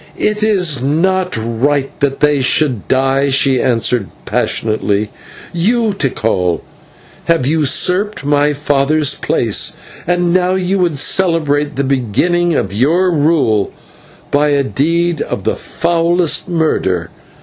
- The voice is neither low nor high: Yes, medium, 150 Hz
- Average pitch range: Yes, average, 4.6 semitones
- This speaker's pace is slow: Yes, slow, 120 wpm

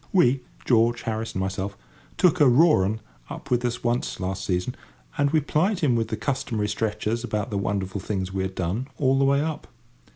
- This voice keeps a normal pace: Yes, average, 190 wpm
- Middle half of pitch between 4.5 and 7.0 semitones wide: Yes, wide, 5.6 semitones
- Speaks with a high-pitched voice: No, low, 115 Hz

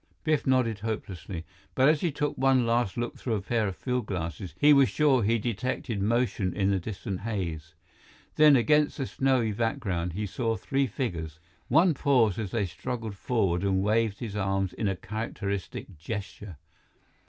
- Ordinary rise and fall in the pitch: Yes, average, 4.7 semitones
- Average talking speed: Yes, average, 170 wpm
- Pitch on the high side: No, low, 110 Hz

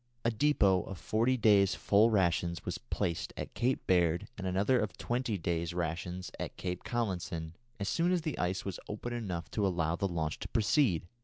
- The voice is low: Yes, very low, 95 Hz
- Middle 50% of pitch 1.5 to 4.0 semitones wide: No, average, 4.7 semitones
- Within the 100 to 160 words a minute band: No, average, 185 wpm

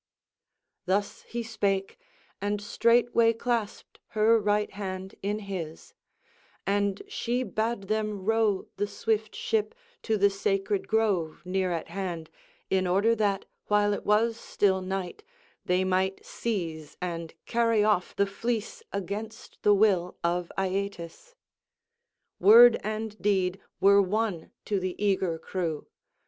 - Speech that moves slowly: Yes, slow, 130 wpm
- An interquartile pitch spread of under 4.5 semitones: Yes, average, 2.7 semitones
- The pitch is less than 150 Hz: No, high, 200 Hz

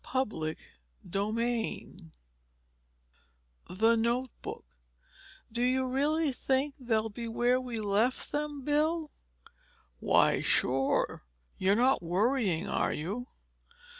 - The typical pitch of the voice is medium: No, high, 240 Hz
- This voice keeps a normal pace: No, slow, 95 wpm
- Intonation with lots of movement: No, average, 4.0 semitones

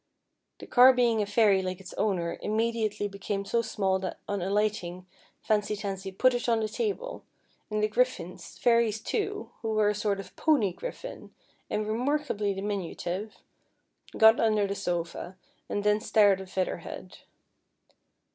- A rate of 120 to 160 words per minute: Yes, average, 155 wpm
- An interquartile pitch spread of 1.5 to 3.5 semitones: Yes, average, 2.9 semitones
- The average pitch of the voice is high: Yes, high, 210 Hz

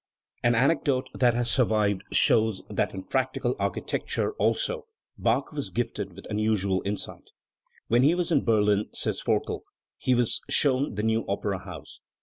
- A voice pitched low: Yes, low, 115 Hz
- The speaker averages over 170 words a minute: No, average, 150 wpm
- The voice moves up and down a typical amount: Yes, average, 4.1 semitones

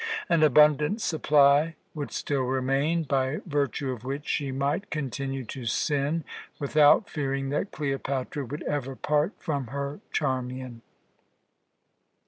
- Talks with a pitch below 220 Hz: Yes, medium, 140 Hz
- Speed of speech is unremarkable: No, slow, 120 wpm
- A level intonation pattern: Yes, narrow, 2.1 semitones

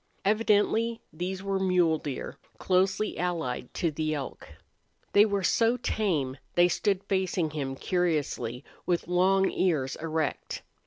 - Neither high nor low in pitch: Yes, medium, 180 Hz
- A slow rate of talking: Yes, slow, 125 wpm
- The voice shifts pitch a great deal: No, average, 3.9 semitones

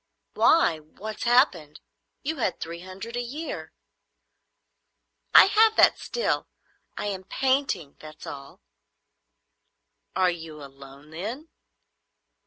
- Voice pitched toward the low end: No, high, 190 Hz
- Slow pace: Yes, slow, 105 wpm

